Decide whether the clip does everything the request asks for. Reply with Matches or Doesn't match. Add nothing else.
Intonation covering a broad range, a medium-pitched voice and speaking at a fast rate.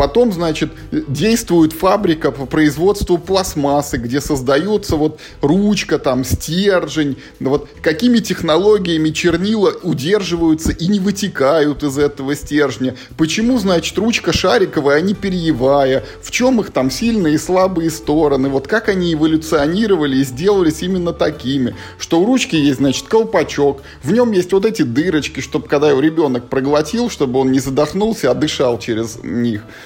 Doesn't match